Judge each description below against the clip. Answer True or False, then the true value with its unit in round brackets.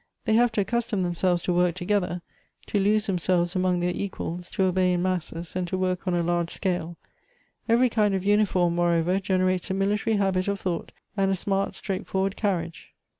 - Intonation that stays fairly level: True (2.1 semitones)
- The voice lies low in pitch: False (185 Hz)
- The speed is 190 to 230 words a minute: True (195 wpm)